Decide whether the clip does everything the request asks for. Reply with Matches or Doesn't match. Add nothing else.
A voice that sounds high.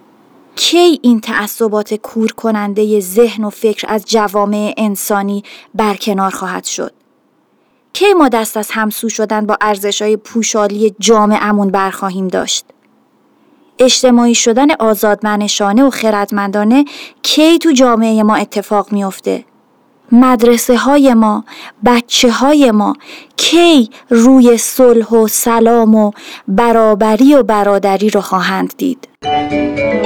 Matches